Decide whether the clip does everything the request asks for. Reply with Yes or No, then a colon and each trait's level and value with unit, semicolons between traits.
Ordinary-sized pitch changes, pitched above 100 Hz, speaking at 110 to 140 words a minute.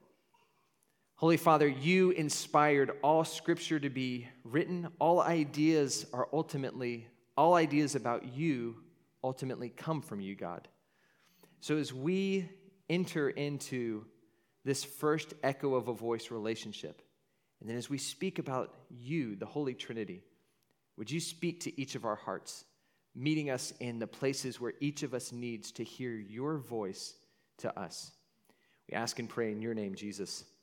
No: average, 4.8 semitones; medium, 140 Hz; average, 150 wpm